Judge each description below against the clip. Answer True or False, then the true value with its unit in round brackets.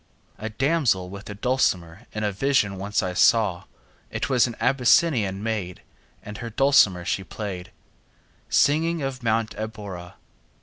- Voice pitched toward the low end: True (110 Hz)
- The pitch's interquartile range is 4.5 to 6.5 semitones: True (4.8 semitones)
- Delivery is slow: False (155 wpm)